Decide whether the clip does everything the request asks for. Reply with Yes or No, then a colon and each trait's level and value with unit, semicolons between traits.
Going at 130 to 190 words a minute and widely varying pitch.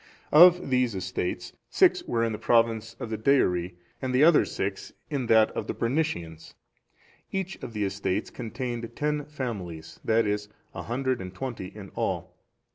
No: average, 165 wpm; average, 5.0 semitones